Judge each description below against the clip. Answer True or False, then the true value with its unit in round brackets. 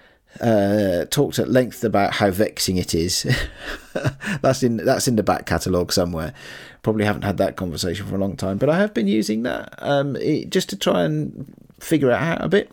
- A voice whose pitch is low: True (110 Hz)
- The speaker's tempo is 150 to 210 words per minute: True (205 wpm)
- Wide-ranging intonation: True (6.4 semitones)